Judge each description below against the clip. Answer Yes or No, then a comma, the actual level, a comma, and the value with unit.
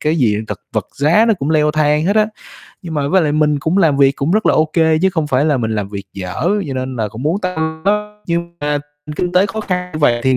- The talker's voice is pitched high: No, medium, 155 Hz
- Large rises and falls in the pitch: No, average, 4.6 semitones